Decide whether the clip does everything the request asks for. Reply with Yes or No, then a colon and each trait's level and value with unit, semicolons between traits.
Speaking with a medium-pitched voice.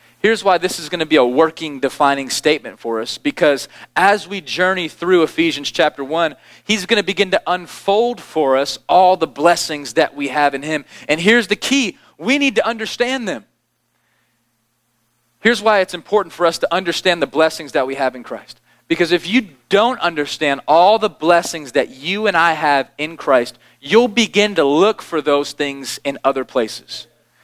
Yes: medium, 165 Hz